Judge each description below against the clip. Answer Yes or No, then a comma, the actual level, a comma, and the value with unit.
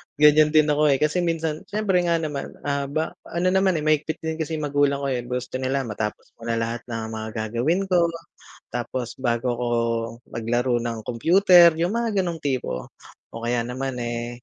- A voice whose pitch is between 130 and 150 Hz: Yes, medium, 140 Hz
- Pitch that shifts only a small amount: No, average, 5.2 semitones